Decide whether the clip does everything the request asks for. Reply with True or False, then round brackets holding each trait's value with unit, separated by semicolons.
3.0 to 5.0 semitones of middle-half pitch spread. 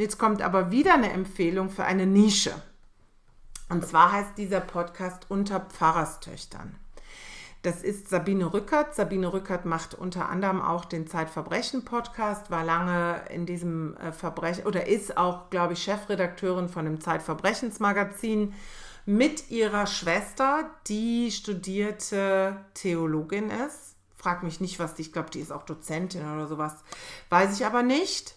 True (3.3 semitones)